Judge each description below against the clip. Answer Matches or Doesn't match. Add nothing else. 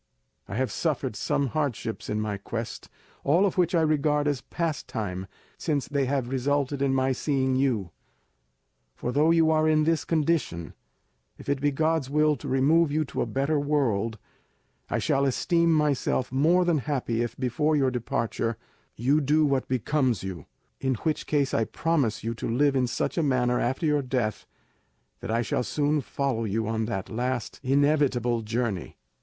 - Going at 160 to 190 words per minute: Matches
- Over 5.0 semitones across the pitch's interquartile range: Doesn't match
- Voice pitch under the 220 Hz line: Matches